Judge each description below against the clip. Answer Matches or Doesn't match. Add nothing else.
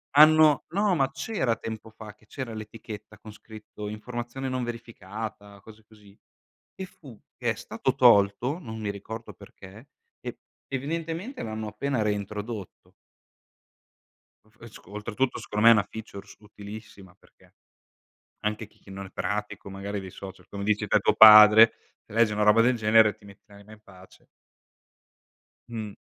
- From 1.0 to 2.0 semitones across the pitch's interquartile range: Doesn't match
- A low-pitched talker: Matches